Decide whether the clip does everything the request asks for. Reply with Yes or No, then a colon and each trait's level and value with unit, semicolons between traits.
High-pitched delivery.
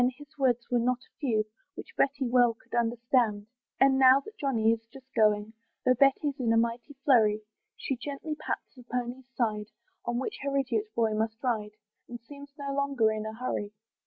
Yes: high, 245 Hz